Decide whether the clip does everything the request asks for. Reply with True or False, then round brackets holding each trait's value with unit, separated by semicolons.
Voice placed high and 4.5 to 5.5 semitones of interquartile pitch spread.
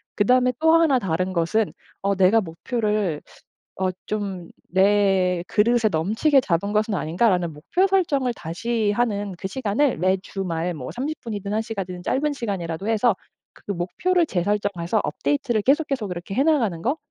True (205 Hz; 5.1 semitones)